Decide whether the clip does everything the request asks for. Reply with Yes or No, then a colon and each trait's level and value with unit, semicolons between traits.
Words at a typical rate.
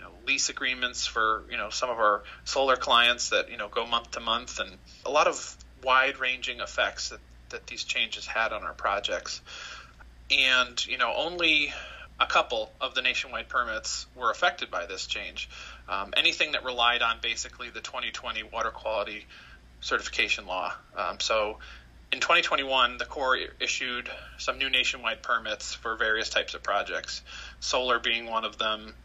Yes: average, 165 wpm